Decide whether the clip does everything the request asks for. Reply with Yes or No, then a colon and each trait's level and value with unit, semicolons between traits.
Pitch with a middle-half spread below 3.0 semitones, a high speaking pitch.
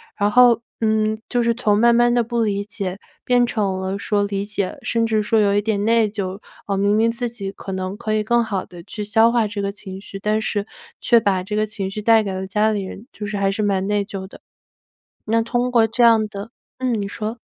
Yes: narrow, 2.4 semitones; high, 210 Hz